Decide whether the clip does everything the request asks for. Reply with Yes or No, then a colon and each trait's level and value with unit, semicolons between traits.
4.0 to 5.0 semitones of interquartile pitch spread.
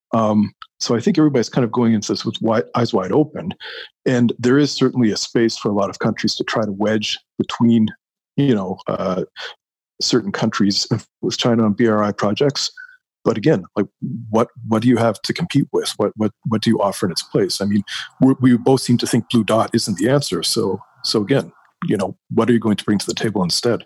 No: average, 3.2 semitones